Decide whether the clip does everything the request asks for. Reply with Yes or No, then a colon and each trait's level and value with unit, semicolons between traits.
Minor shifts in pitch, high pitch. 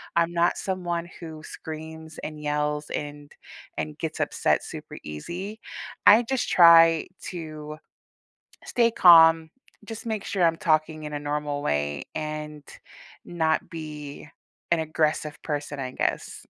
No: narrow, 2.3 semitones; medium, 155 Hz